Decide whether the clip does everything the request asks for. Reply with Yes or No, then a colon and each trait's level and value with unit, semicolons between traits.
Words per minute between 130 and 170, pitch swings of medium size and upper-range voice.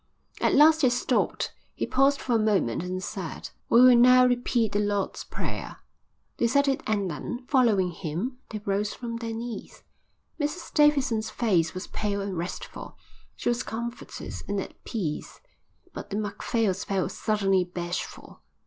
Yes: average, 155 wpm; average, 4.2 semitones; high, 220 Hz